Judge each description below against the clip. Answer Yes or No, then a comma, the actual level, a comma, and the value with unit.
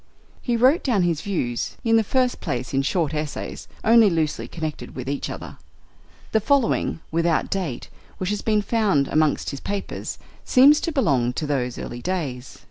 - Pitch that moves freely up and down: Yes, wide, 8.1 semitones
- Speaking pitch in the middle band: Yes, medium, 170 Hz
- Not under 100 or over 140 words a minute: No, average, 170 wpm